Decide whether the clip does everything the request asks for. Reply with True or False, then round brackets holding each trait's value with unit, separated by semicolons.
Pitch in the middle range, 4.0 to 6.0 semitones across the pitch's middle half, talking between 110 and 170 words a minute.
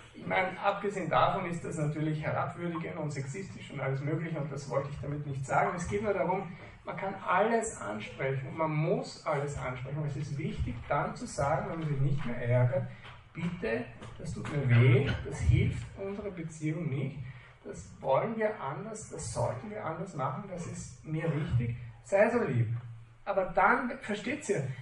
False (150 Hz; 5.4 semitones; 180 wpm)